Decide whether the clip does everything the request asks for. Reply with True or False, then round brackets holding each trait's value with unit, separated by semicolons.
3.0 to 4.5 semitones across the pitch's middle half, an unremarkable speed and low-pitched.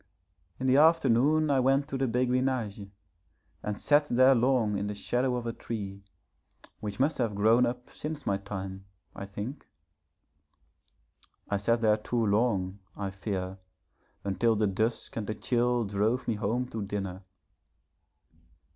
True (4.0 semitones; 145 wpm; 115 Hz)